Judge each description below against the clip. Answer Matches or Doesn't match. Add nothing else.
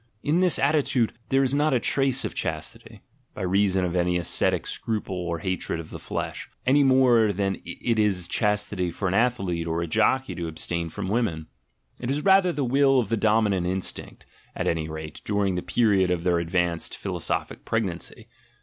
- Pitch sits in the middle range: Doesn't match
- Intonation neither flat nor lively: Doesn't match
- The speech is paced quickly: Doesn't match